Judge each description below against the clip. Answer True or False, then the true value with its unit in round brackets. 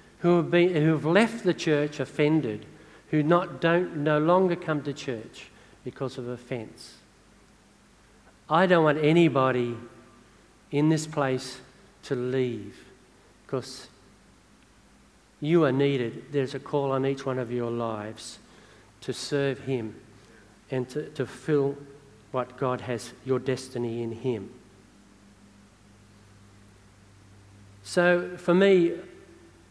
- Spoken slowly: True (125 wpm)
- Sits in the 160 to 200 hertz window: False (130 Hz)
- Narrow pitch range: False (5.3 semitones)